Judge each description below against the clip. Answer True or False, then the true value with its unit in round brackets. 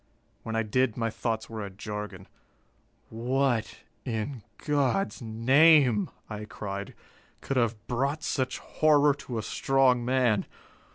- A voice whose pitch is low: True (120 Hz)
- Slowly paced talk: True (125 wpm)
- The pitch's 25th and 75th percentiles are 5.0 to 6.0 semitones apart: False (3.8 semitones)